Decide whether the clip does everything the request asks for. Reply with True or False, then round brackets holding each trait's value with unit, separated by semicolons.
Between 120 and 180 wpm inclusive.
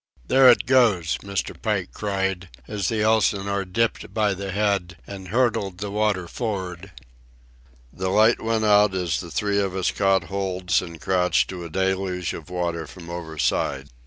True (160 wpm)